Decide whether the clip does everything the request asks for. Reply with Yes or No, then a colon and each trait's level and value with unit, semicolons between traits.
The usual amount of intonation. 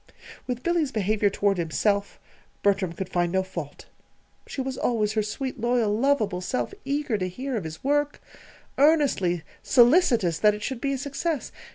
No: wide, 6.2 semitones